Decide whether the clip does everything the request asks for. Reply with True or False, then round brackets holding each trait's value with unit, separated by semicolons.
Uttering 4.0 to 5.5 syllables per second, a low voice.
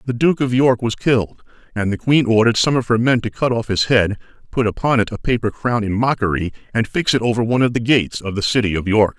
False (6.2 syllables/s; 115 Hz)